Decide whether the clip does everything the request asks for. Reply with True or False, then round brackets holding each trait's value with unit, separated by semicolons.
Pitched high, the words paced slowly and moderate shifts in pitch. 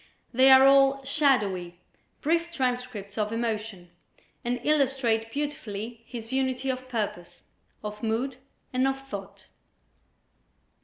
True (245 Hz; 110 wpm; 4.1 semitones)